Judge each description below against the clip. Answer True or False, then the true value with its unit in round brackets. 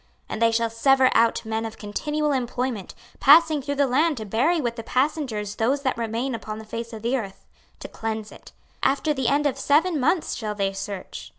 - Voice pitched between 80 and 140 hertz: False (245 Hz)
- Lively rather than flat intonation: False (4.3 semitones)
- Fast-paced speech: True (210 wpm)